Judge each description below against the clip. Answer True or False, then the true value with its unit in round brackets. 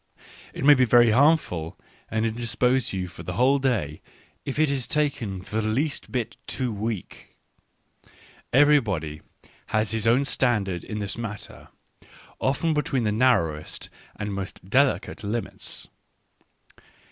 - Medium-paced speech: False (130 wpm)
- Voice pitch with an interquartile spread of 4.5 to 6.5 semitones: True (4.8 semitones)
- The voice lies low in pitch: True (115 Hz)